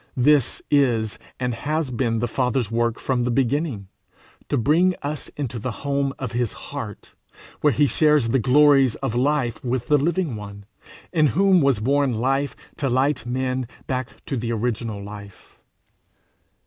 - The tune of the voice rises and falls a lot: No, average, 3.7 semitones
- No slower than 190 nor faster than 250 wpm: No, average, 160 wpm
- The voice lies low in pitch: Yes, low, 130 Hz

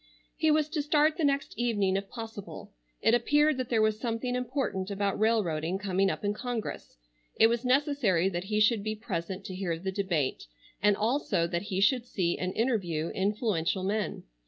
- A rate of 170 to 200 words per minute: Yes, average, 180 wpm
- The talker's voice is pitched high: Yes, high, 210 Hz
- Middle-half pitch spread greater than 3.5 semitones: Yes, average, 4.5 semitones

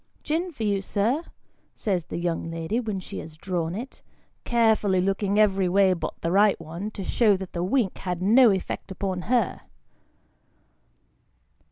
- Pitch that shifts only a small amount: No, average, 3.2 semitones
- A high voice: Yes, high, 195 Hz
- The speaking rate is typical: Yes, average, 170 wpm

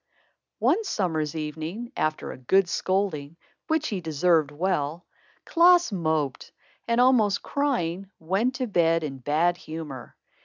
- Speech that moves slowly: Yes, slow, 125 wpm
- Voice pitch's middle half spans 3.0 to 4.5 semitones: No, wide, 5.6 semitones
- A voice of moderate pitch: Yes, medium, 175 Hz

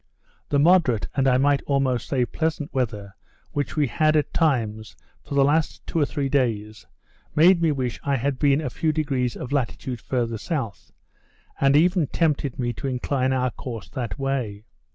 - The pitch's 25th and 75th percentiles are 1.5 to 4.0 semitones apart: Yes, average, 3.3 semitones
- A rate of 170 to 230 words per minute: Yes, average, 175 wpm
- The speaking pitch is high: No, low, 135 Hz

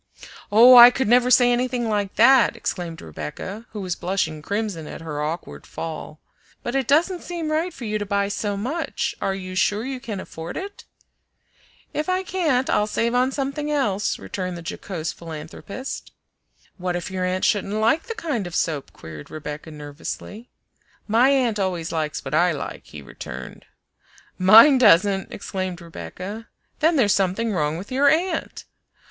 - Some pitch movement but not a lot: No, wide, 6.5 semitones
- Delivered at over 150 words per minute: Yes, average, 165 wpm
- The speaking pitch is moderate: No, high, 205 Hz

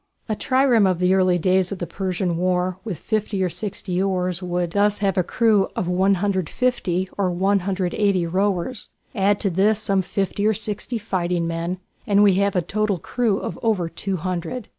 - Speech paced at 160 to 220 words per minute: Yes, average, 175 wpm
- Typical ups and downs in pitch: No, narrow, 2.3 semitones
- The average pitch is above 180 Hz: Yes, high, 190 Hz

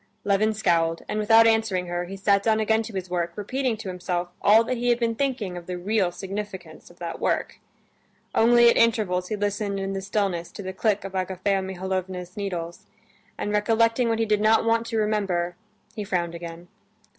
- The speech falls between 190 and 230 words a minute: Yes, average, 195 wpm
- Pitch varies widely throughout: No, average, 3.5 semitones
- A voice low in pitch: No, high, 200 Hz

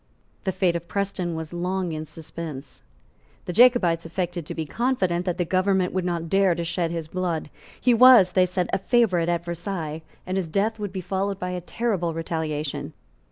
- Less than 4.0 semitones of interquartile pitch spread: Yes, narrow, 2.5 semitones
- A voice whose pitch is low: No, medium, 175 Hz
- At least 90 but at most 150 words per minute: No, average, 190 wpm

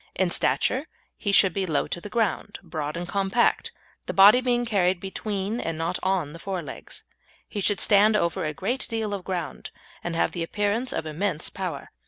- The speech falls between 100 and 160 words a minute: No, average, 195 wpm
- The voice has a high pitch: Yes, high, 195 Hz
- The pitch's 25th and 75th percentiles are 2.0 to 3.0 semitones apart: No, average, 3.6 semitones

